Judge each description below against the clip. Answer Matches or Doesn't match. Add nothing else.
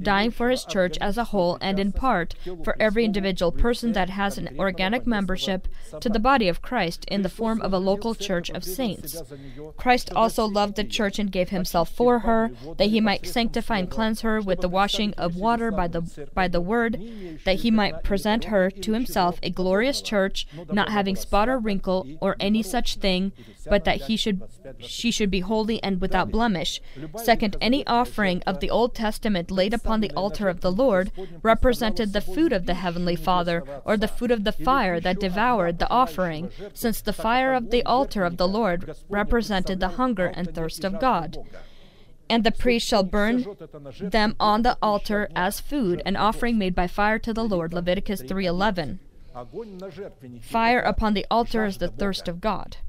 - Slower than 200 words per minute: Matches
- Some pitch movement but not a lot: Matches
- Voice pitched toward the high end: Matches